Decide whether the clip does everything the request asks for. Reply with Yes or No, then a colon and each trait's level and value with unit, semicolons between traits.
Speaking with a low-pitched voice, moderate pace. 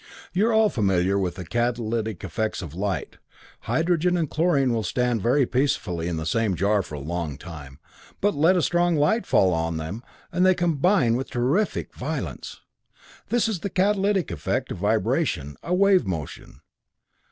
Yes: low, 120 Hz; average, 170 wpm